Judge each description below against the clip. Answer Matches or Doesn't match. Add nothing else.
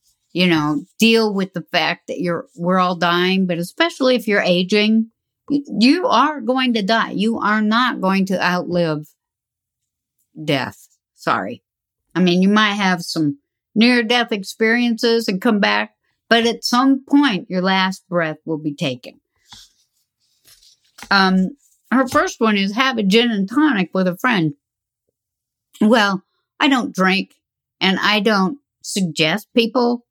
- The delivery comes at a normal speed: Matches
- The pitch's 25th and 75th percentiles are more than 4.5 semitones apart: Matches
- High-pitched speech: Matches